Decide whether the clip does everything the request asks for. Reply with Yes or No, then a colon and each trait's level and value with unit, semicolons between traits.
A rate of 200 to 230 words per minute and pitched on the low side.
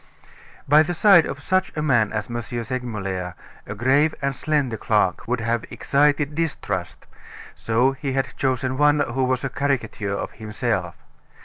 No: average, 155 wpm; low, 130 Hz